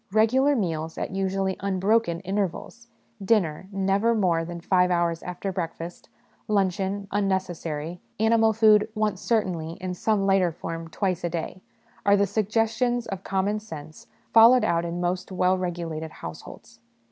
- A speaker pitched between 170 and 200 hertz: Yes, high, 190 Hz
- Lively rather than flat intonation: No, average, 3.6 semitones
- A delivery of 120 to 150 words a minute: Yes, average, 145 wpm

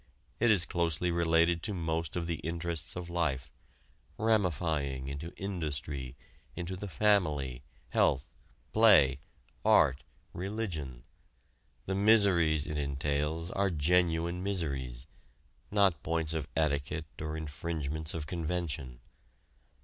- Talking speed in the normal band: No, slow, 110 wpm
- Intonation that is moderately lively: Yes, average, 3.6 semitones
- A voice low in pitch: Yes, very low, 80 Hz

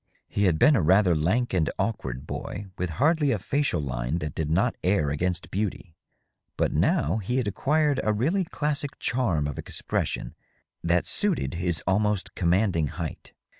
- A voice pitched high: No, very low, 95 Hz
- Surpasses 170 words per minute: No, average, 165 wpm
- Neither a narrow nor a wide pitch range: No, wide, 7.0 semitones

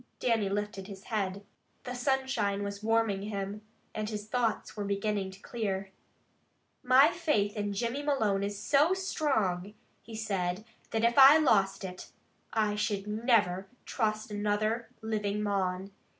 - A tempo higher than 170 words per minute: No, average, 140 wpm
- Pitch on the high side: Yes, high, 210 Hz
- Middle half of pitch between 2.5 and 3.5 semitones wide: Yes, average, 2.8 semitones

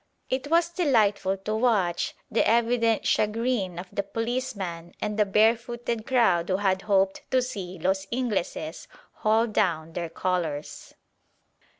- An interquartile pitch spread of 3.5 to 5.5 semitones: Yes, average, 4.1 semitones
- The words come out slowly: Yes, slow, 130 wpm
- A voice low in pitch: No, high, 210 Hz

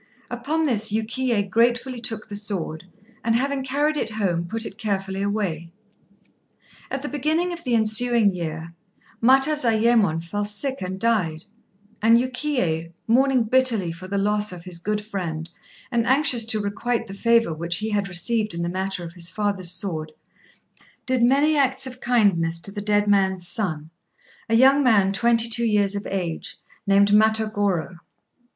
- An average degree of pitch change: Yes, average, 4.4 semitones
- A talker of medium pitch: No, high, 210 Hz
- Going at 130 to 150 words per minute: No, average, 160 wpm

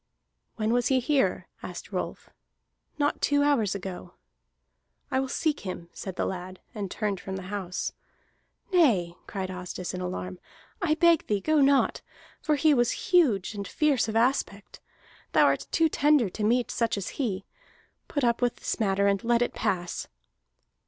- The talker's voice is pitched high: Yes, high, 225 Hz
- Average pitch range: No, wide, 6.7 semitones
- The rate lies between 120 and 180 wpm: Yes, average, 165 wpm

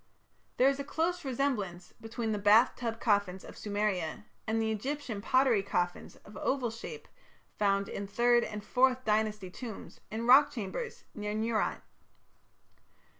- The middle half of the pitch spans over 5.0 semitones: No, average, 3.8 semitones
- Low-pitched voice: No, high, 220 Hz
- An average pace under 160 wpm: Yes, average, 145 wpm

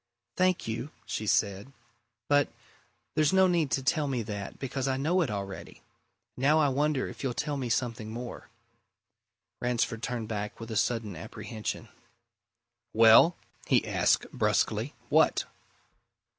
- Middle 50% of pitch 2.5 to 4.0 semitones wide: No, average, 4.6 semitones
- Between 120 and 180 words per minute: Yes, average, 140 wpm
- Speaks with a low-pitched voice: Yes, low, 125 Hz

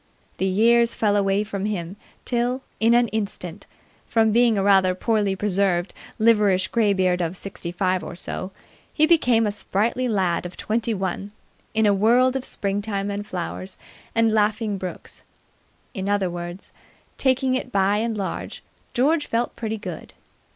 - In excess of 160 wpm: No, average, 155 wpm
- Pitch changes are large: No, average, 3.3 semitones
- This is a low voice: No, high, 205 Hz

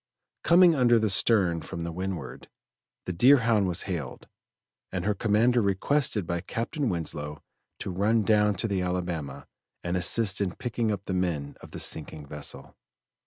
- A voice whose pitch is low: Yes, very low, 95 Hz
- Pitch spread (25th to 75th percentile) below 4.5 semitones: No, average, 4.8 semitones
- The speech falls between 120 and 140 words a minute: No, average, 160 wpm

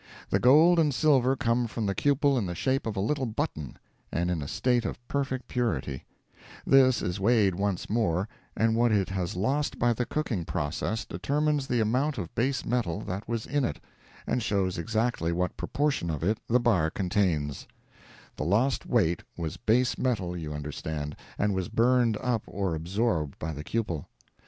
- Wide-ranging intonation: Yes, wide, 6.2 semitones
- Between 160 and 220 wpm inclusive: Yes, average, 175 wpm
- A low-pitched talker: Yes, low, 110 Hz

